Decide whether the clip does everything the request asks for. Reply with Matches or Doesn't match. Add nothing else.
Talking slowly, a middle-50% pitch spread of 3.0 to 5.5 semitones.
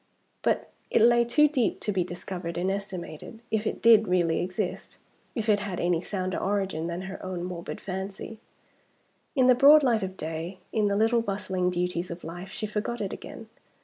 Doesn't match